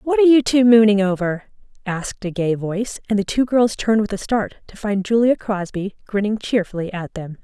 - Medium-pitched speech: No, high, 210 Hz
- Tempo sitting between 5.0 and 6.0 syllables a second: Yes, 5.6 syllables/s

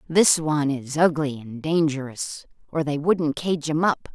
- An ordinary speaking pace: Yes, average, 175 wpm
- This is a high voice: No, medium, 150 Hz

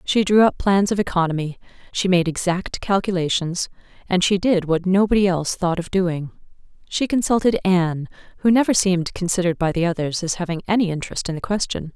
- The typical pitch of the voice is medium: Yes, medium, 180 Hz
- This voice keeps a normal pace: Yes, average, 180 wpm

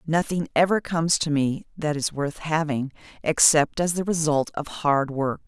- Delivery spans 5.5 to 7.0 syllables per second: No, 4.6 syllables/s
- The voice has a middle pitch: Yes, medium, 155 Hz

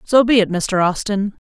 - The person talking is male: No, female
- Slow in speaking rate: No, fast, 205 wpm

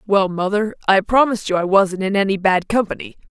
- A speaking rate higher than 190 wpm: Yes, average, 200 wpm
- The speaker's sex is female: Yes, female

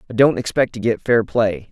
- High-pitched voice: No, low, 115 Hz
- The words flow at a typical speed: No, fast, 245 wpm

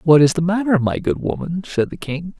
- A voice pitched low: No, medium, 165 Hz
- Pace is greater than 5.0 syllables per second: Yes, 5.5 syllables/s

